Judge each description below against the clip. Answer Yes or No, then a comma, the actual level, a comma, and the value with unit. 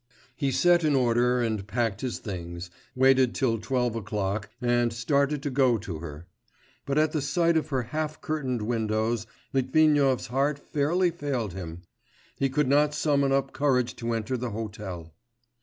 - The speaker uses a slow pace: No, average, 160 wpm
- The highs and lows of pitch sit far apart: No, average, 4.4 semitones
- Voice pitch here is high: No, low, 125 Hz